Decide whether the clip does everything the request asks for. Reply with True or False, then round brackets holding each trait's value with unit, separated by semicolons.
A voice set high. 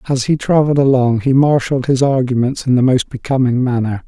False (130 Hz)